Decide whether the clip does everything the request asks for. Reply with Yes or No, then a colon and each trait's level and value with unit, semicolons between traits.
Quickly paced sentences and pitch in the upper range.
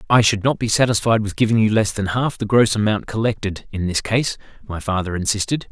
No: fast, 210 wpm; low, 110 Hz